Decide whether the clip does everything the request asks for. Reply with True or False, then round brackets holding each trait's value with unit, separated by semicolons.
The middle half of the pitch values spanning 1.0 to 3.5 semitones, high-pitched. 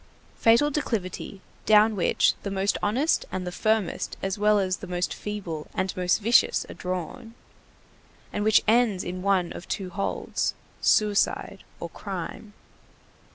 True (2.9 semitones; 200 Hz)